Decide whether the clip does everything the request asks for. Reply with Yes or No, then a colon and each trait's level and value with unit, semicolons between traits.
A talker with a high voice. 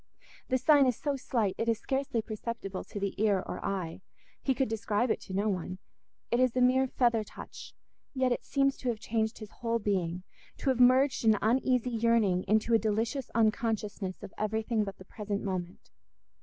Yes: high, 225 Hz